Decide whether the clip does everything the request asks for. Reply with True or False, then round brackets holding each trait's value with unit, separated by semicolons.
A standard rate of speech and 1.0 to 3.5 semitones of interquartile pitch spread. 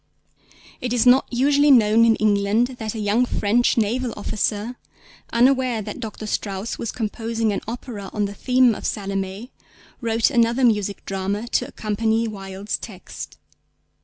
True (145 wpm; 2.9 semitones)